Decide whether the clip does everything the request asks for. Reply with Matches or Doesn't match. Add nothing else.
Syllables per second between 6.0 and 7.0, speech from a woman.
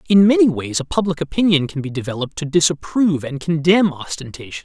Doesn't match